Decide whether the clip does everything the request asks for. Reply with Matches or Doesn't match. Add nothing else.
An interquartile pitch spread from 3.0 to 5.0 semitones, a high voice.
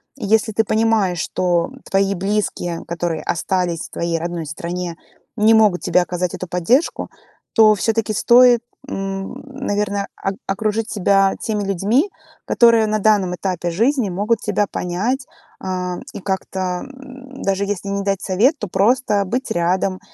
Matches